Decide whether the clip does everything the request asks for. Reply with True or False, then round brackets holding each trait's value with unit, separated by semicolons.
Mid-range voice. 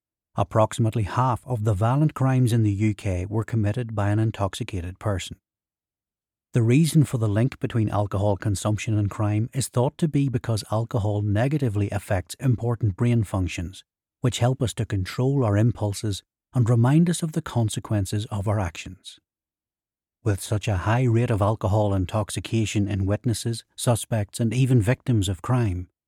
False (110 Hz)